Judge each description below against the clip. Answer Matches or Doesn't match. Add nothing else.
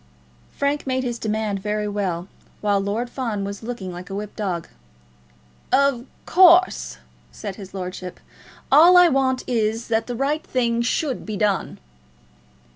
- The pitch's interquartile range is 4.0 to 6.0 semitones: Matches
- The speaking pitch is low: Doesn't match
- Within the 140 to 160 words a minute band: Matches